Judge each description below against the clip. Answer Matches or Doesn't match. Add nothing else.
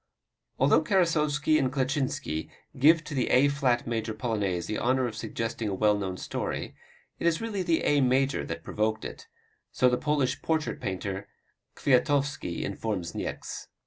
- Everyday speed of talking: Matches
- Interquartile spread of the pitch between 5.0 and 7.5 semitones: Matches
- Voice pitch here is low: Matches